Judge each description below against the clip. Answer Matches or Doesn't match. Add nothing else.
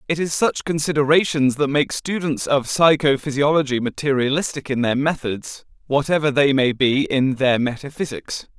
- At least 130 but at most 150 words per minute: Matches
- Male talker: Matches